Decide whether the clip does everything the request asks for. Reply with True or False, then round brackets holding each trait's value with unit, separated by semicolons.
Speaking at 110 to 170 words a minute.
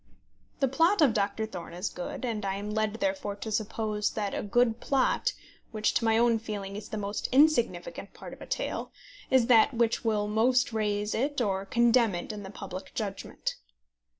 False (195 wpm)